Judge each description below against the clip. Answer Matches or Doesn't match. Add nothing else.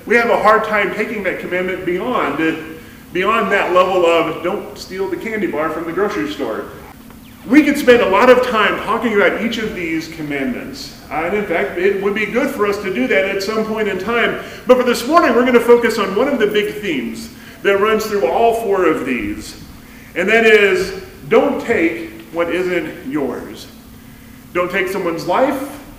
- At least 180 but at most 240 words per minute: Matches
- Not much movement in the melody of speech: Doesn't match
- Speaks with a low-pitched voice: Doesn't match